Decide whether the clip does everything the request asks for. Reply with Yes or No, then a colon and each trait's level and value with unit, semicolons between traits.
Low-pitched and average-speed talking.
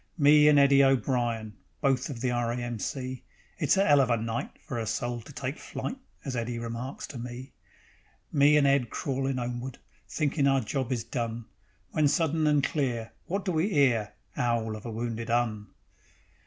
Yes: low, 125 Hz; average, 185 wpm